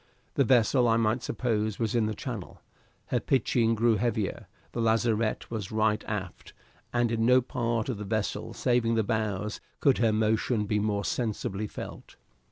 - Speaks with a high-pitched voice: No, low, 110 Hz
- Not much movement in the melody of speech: Yes, narrow, 1.8 semitones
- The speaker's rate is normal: Yes, average, 170 wpm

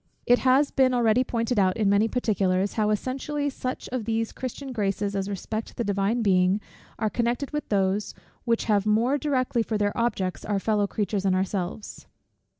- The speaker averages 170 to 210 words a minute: Yes, average, 175 wpm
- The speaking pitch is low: No, high, 215 Hz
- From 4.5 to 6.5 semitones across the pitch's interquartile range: No, average, 3.6 semitones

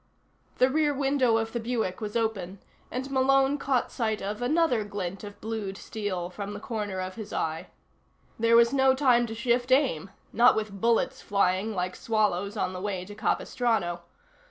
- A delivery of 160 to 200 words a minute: Yes, average, 175 wpm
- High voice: Yes, high, 220 Hz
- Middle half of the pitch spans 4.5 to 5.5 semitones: No, average, 3.8 semitones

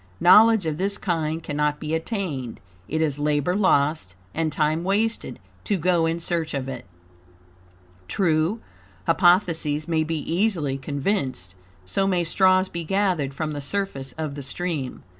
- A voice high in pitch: No, medium, 160 Hz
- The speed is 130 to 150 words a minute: Yes, average, 145 wpm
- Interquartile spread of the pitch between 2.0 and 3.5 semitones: No, average, 4.1 semitones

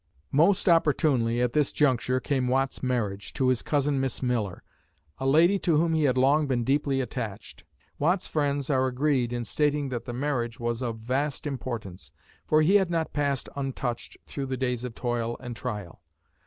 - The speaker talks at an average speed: Yes, average, 180 wpm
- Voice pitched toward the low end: Yes, low, 130 Hz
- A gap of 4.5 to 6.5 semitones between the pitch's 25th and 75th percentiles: No, average, 3.4 semitones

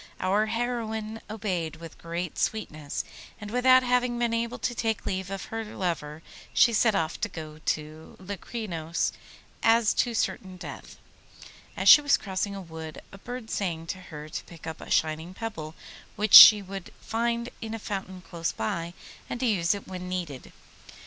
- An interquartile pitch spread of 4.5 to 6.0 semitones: Yes, average, 5.2 semitones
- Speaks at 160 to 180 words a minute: Yes, average, 170 wpm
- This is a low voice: No, high, 195 Hz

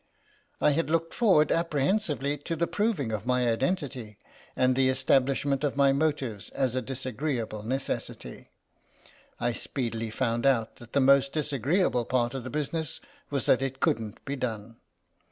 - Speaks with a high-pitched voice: No, low, 135 Hz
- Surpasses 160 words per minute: No, average, 155 wpm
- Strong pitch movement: No, average, 3.6 semitones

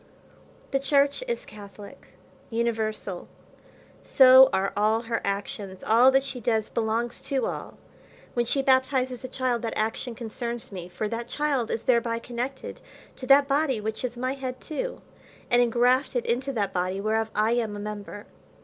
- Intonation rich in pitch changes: No, average, 3.2 semitones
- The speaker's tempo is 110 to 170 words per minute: Yes, average, 165 wpm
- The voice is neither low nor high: No, high, 235 Hz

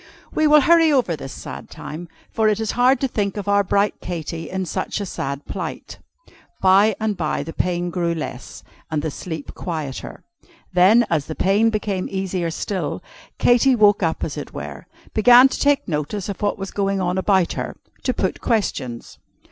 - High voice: Yes, high, 195 Hz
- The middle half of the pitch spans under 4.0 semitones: No, average, 4.3 semitones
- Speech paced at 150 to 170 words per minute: No, average, 180 wpm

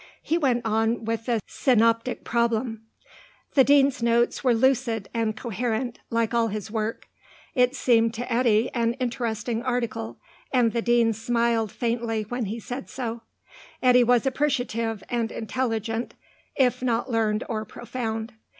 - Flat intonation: Yes, narrow, 1.7 semitones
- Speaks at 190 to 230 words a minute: No, average, 140 wpm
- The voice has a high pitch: Yes, high, 235 Hz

